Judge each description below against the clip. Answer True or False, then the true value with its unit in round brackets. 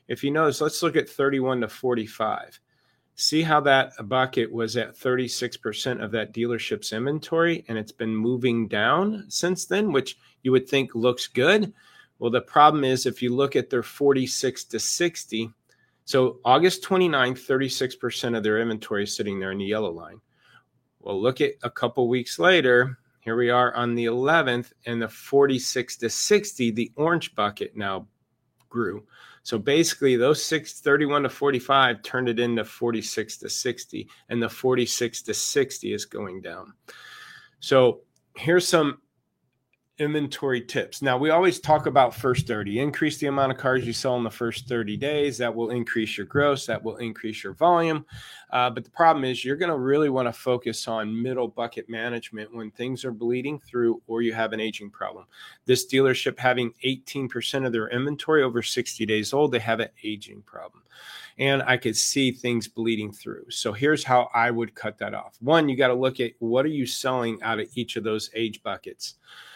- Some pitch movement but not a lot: True (3.4 semitones)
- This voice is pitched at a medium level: False (125 Hz)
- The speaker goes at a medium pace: True (185 wpm)